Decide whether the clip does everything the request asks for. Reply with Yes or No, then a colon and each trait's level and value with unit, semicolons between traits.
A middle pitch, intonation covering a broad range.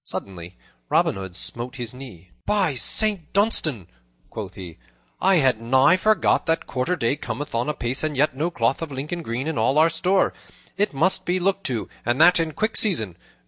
Yes: medium, 145 Hz; wide, 7.0 semitones